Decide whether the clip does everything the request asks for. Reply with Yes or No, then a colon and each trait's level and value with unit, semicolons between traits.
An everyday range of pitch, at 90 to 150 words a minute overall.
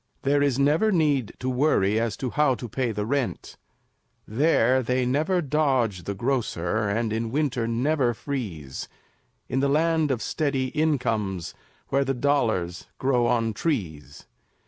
Yes: average, 4.4 semitones; average, 145 wpm